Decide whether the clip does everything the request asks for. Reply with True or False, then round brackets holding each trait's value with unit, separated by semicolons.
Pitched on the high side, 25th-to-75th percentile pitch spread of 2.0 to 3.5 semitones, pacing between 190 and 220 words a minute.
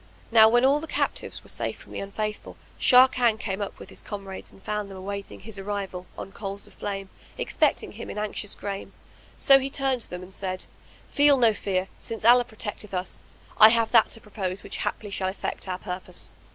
True (205 Hz; 2.8 semitones; 205 wpm)